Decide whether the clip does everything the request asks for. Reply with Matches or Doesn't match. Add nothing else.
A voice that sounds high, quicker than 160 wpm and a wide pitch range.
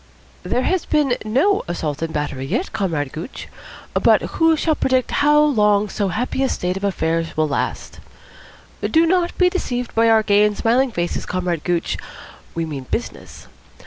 Matches